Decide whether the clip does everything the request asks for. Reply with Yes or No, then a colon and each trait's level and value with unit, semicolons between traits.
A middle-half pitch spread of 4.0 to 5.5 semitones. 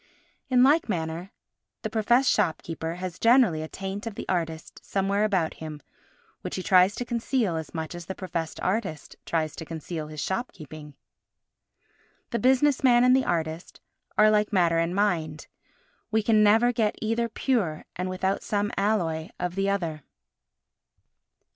Yes: average, 5.2 semitones